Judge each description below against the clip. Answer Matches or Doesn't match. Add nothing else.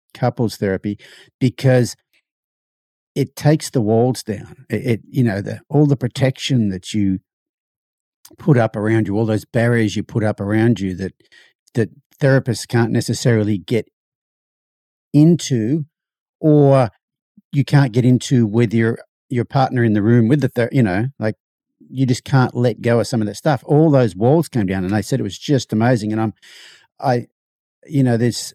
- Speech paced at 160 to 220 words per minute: Matches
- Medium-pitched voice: Doesn't match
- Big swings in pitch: Doesn't match